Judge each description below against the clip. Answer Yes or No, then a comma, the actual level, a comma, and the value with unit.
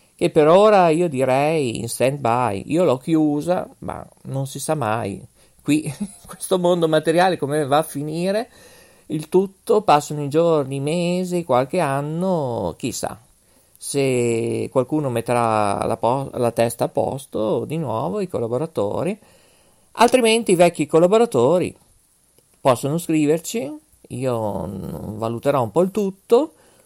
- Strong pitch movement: Yes, wide, 6.0 semitones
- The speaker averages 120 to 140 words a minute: Yes, average, 135 wpm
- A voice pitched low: No, medium, 150 Hz